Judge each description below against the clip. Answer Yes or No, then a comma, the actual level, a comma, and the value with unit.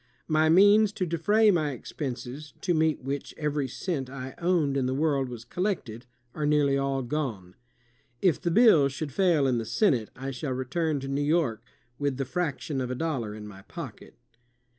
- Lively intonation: No, average, 4.0 semitones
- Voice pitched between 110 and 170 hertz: Yes, medium, 140 Hz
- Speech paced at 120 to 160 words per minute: No, average, 185 wpm